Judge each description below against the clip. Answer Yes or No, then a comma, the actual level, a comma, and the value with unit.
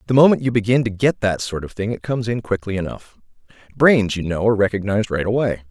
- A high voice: No, low, 110 Hz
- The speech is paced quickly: Yes, fast, 230 wpm